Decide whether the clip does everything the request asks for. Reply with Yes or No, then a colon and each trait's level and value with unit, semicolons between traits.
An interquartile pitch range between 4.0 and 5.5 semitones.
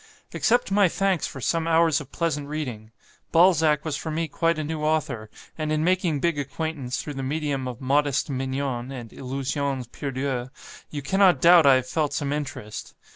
No: average, 3.4 semitones